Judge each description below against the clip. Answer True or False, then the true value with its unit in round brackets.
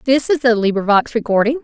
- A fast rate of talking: False (185 wpm)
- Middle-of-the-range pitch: False (240 Hz)